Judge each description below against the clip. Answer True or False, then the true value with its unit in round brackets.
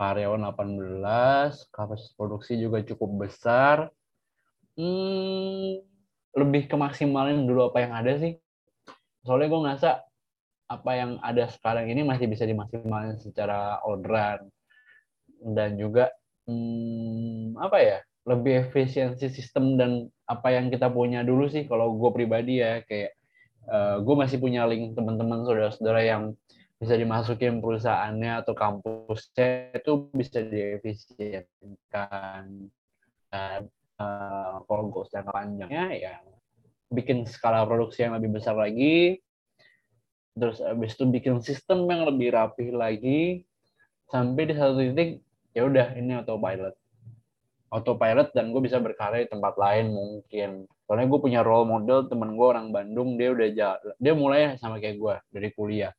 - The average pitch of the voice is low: True (115 Hz)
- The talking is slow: False (130 wpm)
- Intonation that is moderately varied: True (3.6 semitones)